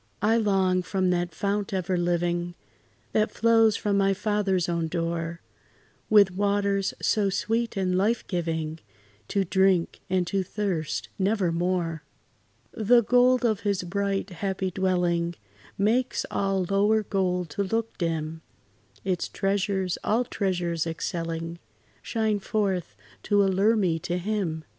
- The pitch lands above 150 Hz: Yes, high, 190 Hz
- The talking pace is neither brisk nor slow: No, slow, 130 wpm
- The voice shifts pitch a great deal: No, average, 2.9 semitones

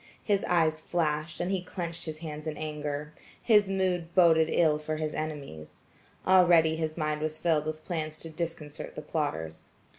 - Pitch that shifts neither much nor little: No, narrow, 2.0 semitones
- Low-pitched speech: No, medium, 155 Hz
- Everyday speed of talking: Yes, average, 170 wpm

